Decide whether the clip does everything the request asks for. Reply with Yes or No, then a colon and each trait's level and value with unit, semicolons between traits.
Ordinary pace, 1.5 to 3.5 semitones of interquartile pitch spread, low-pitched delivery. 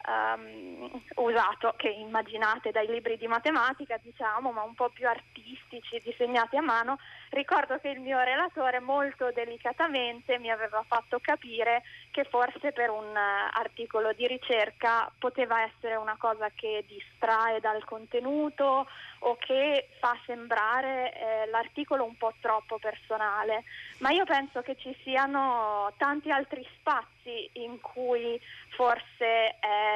No: average, 130 wpm; average, 2.9 semitones; high, 240 Hz